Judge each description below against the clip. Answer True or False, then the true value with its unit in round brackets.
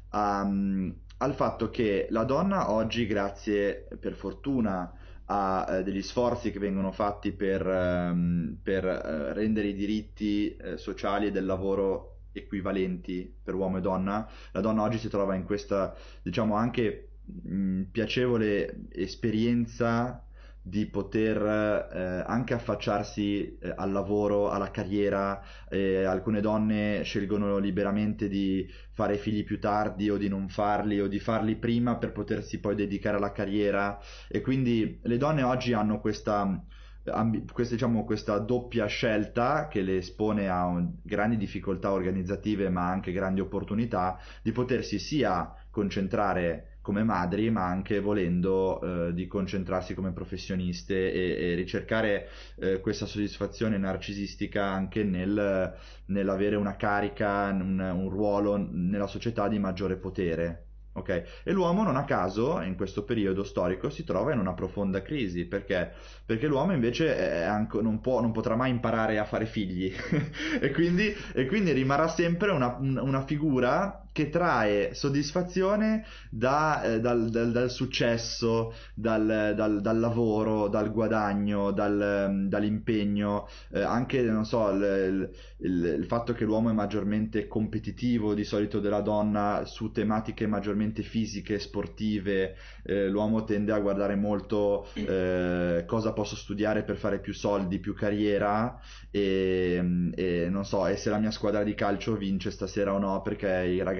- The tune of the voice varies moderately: False (2.3 semitones)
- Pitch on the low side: True (105 Hz)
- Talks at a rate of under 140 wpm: False (145 wpm)